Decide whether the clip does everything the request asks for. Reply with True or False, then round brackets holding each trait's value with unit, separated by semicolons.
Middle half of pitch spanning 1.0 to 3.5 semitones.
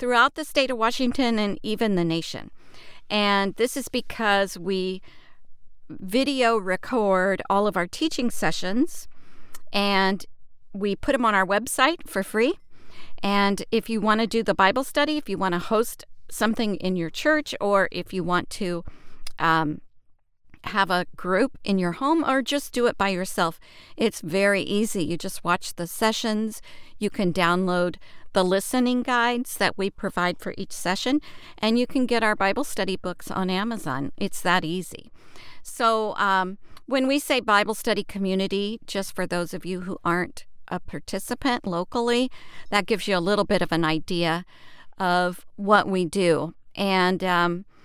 False (4.1 semitones)